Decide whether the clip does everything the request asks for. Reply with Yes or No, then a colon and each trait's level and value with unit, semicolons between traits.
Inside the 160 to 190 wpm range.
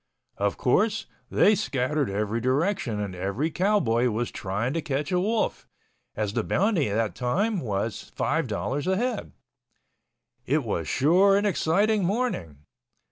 No: slow, 135 wpm